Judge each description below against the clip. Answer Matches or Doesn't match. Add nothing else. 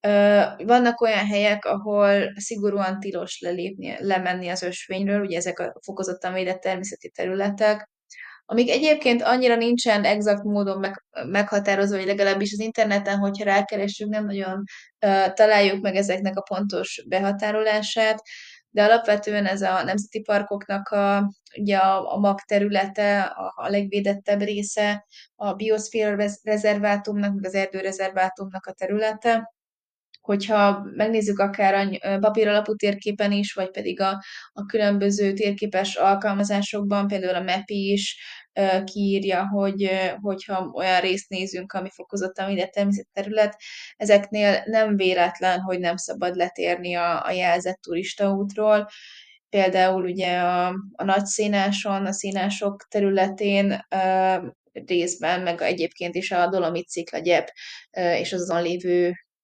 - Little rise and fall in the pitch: Matches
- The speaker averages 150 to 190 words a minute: Doesn't match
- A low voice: Doesn't match